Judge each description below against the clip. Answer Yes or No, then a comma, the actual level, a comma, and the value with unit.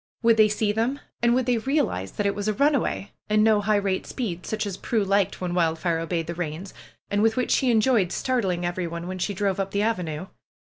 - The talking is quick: Yes, fast, 230 wpm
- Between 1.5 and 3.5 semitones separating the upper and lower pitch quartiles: No, average, 4.0 semitones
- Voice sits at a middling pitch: No, high, 200 Hz